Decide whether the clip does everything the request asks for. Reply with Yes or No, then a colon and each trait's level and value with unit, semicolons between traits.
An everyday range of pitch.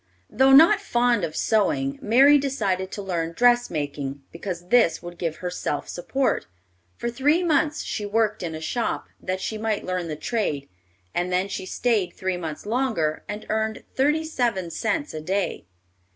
No: wide, 5.9 semitones